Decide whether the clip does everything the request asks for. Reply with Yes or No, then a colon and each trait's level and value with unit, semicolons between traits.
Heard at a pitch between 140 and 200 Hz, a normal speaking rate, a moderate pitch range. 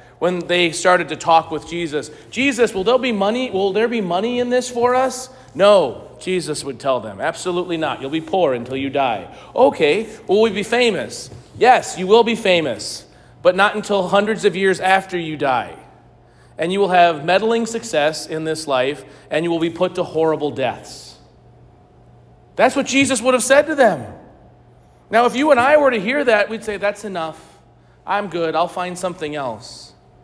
No: medium, 185 Hz; average, 190 wpm; wide, 6.2 semitones